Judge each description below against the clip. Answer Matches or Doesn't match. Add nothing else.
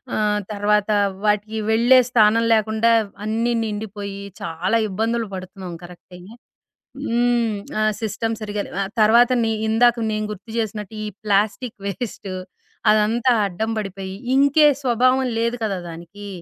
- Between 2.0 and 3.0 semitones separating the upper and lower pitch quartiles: Matches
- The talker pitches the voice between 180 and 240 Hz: Matches